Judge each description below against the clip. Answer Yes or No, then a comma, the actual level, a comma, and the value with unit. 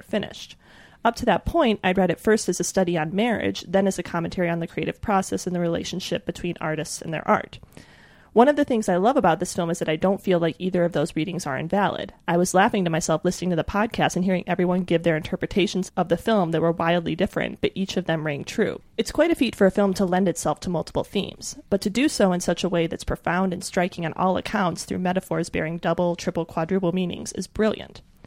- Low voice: No, medium, 180 Hz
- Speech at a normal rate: No, fast, 245 wpm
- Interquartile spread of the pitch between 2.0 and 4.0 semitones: Yes, narrow, 2.4 semitones